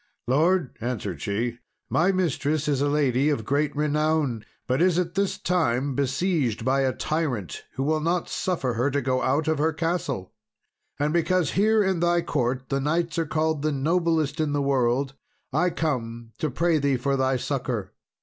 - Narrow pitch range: No, average, 4.1 semitones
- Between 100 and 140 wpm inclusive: No, average, 180 wpm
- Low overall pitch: No, medium, 145 Hz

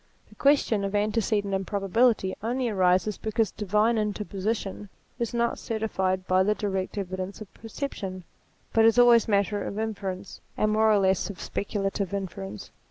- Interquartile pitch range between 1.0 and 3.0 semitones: Yes, narrow, 2.5 semitones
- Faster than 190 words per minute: No, average, 155 wpm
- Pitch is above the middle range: Yes, high, 205 Hz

